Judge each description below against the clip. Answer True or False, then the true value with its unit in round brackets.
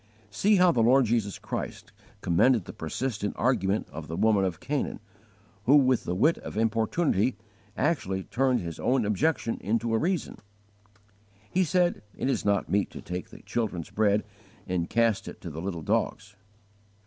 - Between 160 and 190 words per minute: True (165 wpm)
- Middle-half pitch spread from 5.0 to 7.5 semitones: True (5.3 semitones)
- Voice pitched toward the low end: True (110 Hz)